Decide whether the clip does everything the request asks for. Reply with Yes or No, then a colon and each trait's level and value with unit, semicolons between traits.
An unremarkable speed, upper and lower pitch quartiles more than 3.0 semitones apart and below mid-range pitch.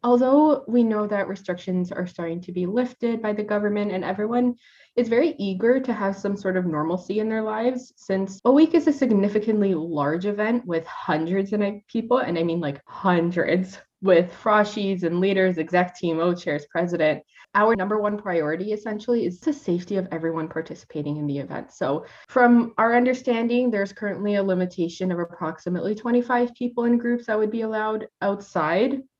No: average, 175 wpm; average, 4.9 semitones; high, 200 Hz